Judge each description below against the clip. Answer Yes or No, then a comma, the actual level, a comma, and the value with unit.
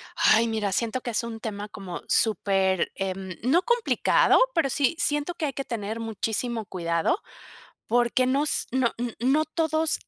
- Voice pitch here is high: Yes, high, 235 Hz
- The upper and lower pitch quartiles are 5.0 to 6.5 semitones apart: Yes, average, 5.3 semitones